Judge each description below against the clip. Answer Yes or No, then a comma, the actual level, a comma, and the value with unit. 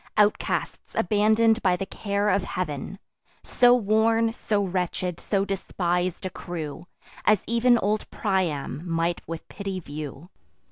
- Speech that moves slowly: Yes, slow, 130 wpm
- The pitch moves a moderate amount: Yes, average, 3.5 semitones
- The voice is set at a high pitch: Yes, high, 195 Hz